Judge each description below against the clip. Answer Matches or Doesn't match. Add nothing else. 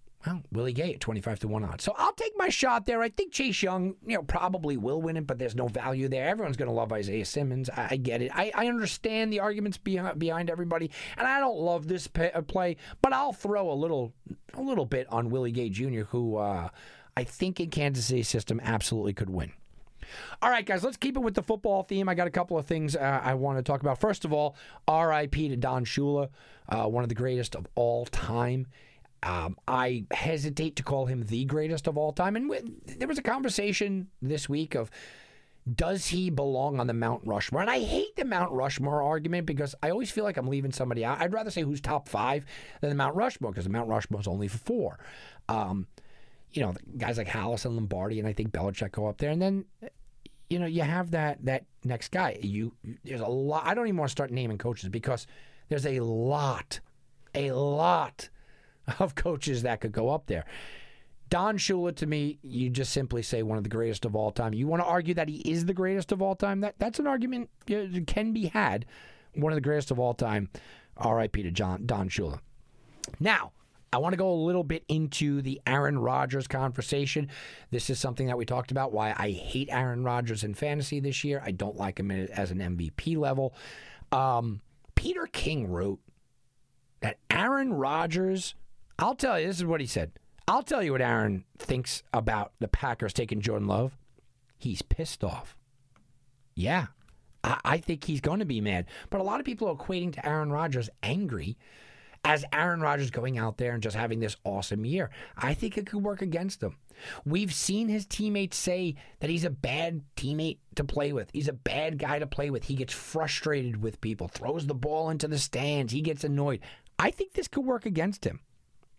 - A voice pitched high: Doesn't match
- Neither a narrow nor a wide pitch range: Doesn't match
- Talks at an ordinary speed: Doesn't match